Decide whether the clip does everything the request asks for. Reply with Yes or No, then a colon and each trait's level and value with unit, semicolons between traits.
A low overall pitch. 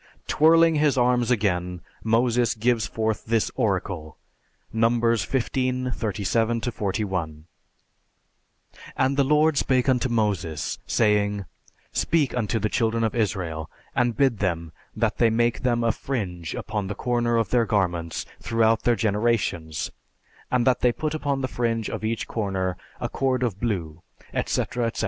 Yes: low, 115 Hz